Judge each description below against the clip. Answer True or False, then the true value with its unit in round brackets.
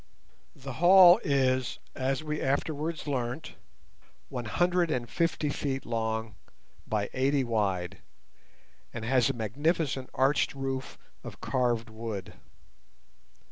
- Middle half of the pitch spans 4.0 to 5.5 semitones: True (4.3 semitones)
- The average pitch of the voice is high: False (130 Hz)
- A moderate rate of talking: False (110 wpm)